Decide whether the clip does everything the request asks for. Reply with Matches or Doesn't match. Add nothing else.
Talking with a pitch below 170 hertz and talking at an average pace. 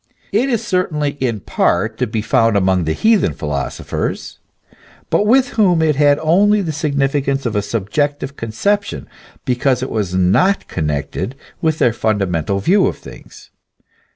Matches